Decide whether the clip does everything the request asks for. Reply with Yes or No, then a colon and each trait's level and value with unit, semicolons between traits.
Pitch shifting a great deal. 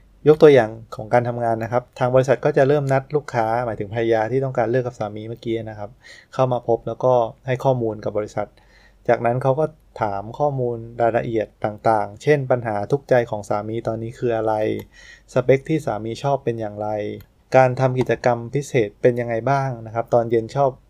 No: average, 2.8 semitones